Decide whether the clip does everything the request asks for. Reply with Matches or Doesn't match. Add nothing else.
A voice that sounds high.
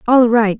Matches